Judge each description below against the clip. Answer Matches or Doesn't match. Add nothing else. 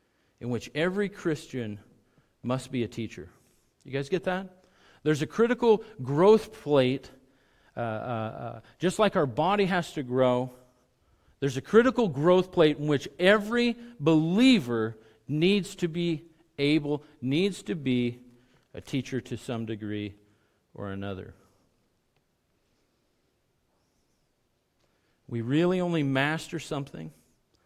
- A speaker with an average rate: Doesn't match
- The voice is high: Doesn't match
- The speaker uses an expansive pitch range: Matches